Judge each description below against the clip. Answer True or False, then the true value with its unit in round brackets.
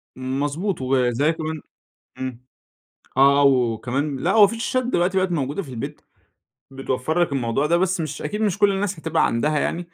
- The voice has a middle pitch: True (150 Hz)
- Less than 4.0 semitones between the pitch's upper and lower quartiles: False (5.2 semitones)